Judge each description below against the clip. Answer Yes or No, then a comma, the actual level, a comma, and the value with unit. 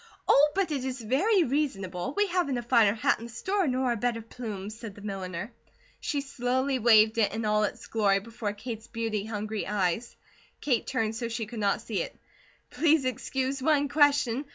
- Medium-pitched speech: No, high, 235 Hz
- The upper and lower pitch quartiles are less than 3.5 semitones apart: No, average, 4.1 semitones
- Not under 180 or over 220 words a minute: Yes, average, 190 wpm